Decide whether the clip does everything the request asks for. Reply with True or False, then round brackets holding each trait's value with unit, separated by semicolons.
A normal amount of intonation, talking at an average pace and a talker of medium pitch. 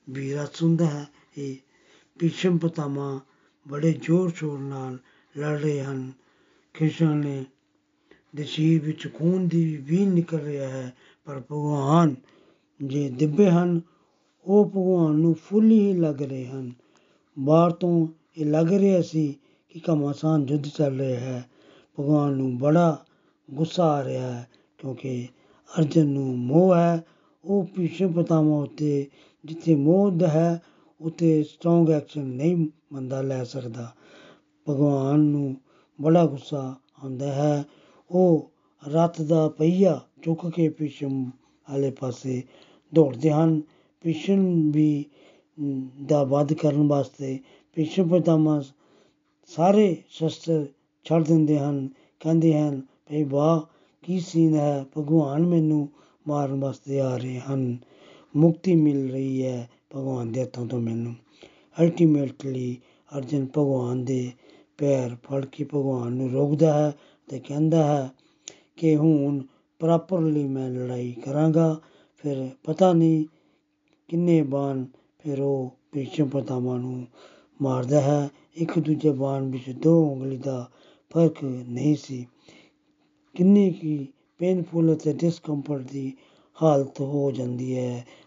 True (3.2 semitones; 115 wpm; 150 Hz)